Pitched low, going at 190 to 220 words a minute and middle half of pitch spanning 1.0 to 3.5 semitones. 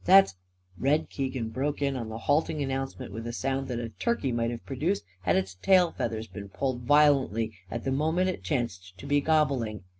No: low, 130 Hz; fast, 205 wpm; average, 4.6 semitones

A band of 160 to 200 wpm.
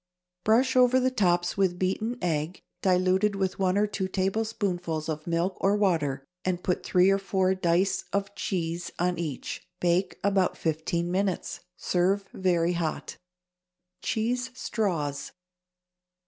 No: slow, 135 wpm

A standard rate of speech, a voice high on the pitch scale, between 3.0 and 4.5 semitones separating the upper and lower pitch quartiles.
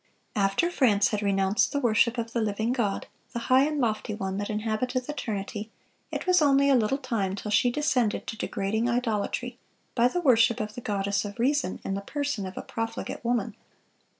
Yes: average, 195 wpm; high, 225 Hz; average, 3.7 semitones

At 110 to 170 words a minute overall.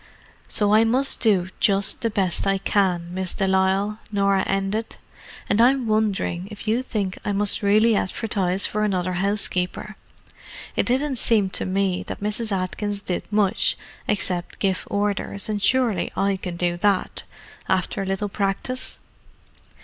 Yes: average, 150 wpm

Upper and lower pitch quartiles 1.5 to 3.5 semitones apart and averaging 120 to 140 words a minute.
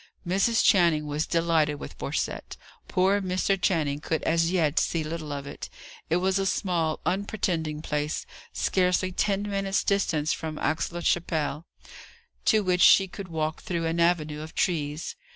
No: average, 3.2 semitones; average, 155 wpm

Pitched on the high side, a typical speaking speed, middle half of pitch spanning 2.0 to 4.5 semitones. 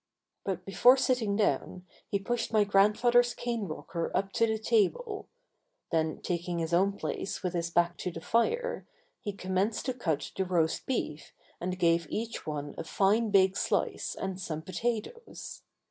No: high, 195 Hz; average, 160 wpm; average, 4.9 semitones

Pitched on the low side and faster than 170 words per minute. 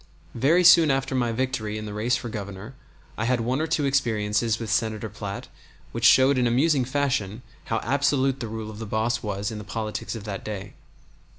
Yes: low, 115 Hz; average, 200 wpm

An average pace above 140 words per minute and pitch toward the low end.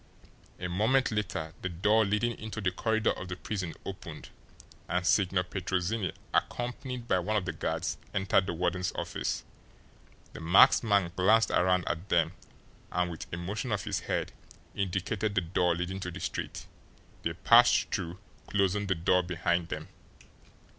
Yes: average, 160 wpm; very low, 95 Hz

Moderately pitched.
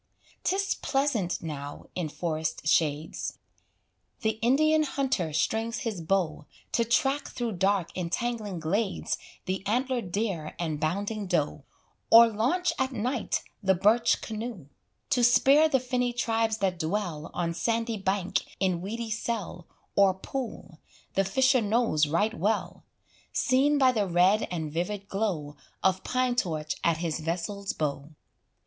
No: high, 205 Hz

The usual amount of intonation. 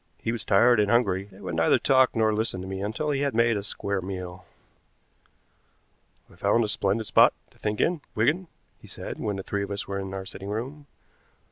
Yes: average, 3.4 semitones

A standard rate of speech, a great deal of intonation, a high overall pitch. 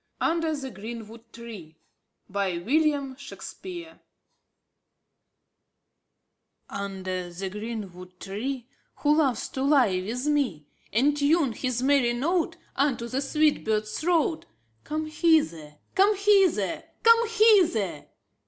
No: slow, 125 wpm; wide, 7.7 semitones; very high, 255 Hz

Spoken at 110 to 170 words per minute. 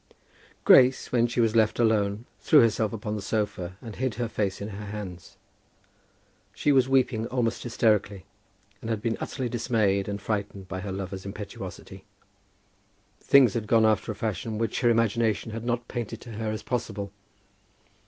Yes: average, 165 wpm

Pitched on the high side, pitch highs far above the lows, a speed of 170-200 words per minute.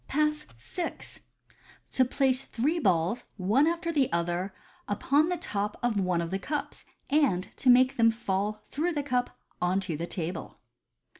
No: high, 235 Hz; wide, 7.5 semitones; average, 160 wpm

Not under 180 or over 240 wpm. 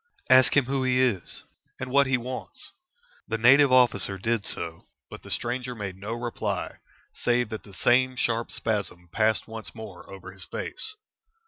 No: average, 165 wpm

